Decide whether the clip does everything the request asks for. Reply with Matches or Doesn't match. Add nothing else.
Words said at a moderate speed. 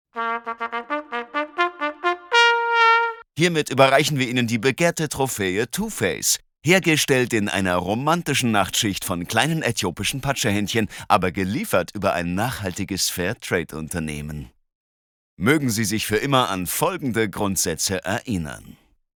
Doesn't match